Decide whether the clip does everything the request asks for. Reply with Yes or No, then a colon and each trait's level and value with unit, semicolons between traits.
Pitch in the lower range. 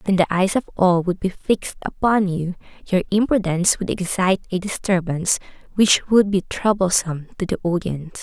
No: medium, 185 Hz